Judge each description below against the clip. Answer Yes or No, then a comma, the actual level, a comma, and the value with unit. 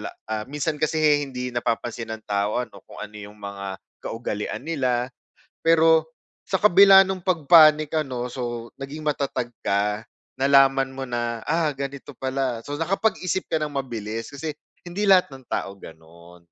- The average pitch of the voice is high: No, low, 135 Hz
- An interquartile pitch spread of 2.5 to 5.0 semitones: No, wide, 5.4 semitones